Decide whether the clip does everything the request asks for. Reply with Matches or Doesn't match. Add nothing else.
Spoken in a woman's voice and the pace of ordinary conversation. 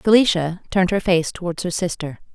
Matches